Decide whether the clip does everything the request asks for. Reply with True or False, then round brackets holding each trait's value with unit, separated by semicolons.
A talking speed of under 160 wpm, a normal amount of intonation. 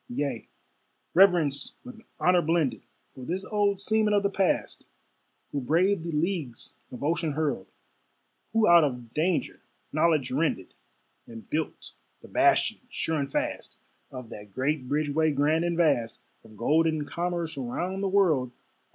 True (140 wpm; 4.7 semitones)